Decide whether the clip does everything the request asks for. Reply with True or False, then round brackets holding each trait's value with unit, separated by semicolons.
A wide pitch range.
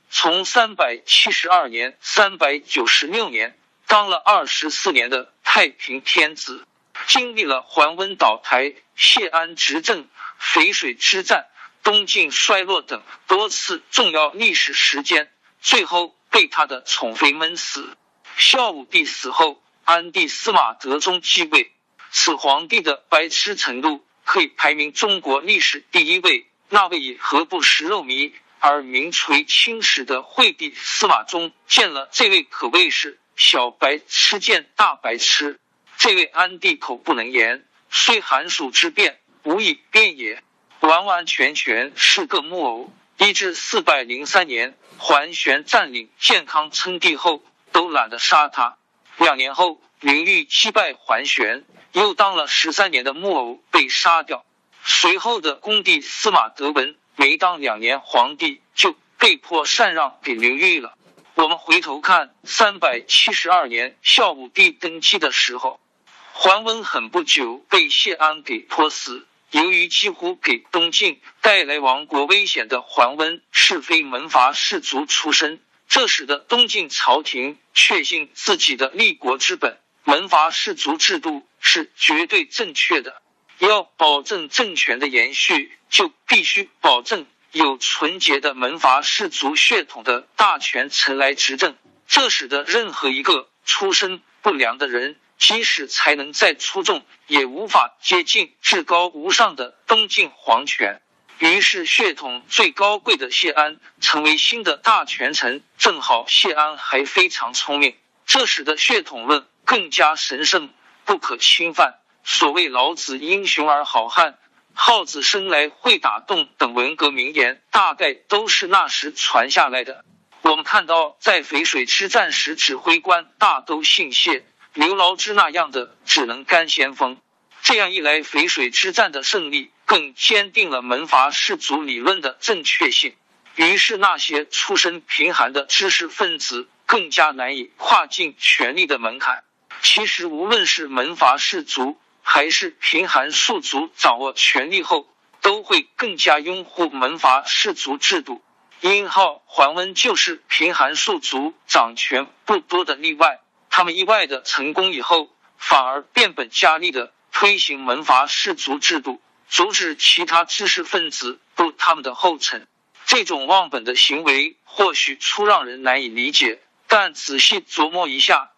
True (6.1 semitones)